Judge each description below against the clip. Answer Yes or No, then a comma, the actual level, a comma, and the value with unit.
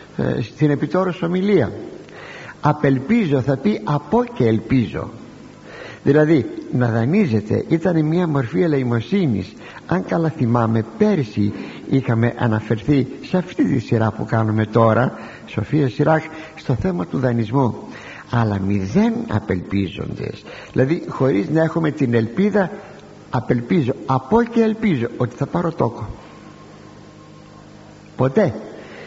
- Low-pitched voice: Yes, low, 130 Hz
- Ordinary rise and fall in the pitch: No, wide, 6.4 semitones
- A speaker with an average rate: No, slow, 110 wpm